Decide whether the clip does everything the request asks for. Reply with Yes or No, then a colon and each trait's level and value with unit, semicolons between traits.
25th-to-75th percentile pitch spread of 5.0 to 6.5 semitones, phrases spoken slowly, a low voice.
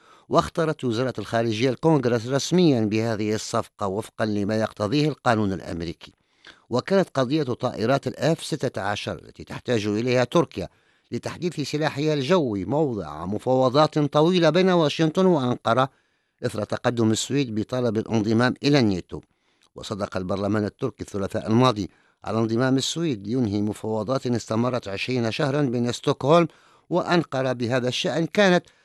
Yes: wide, 5.5 semitones; slow, 115 wpm; low, 125 Hz